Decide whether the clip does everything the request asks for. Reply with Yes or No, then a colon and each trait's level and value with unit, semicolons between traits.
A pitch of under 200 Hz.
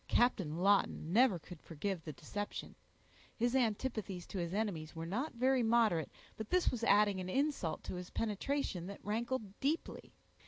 No: high, 205 Hz